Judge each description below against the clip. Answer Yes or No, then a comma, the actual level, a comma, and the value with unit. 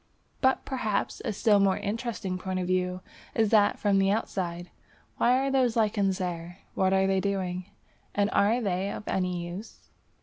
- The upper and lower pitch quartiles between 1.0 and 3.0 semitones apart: Yes, average, 2.7 semitones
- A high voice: Yes, high, 195 Hz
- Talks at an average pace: Yes, average, 170 wpm